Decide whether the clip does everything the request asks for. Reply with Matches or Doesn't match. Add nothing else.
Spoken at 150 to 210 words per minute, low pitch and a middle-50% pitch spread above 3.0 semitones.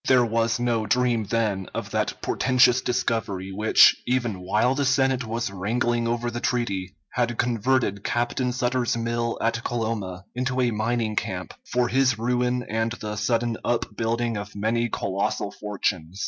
Doesn't match